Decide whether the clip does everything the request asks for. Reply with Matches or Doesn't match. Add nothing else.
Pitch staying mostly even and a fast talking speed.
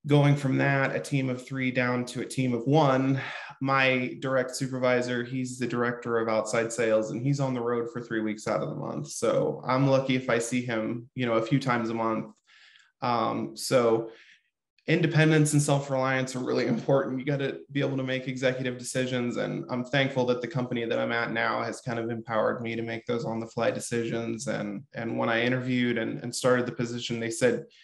Matches